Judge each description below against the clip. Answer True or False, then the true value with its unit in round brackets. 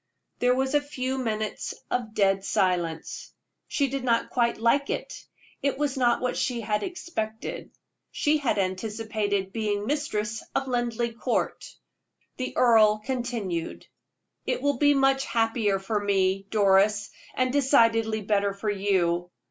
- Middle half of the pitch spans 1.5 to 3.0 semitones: False (4.1 semitones)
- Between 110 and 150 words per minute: True (140 wpm)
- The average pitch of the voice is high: True (225 Hz)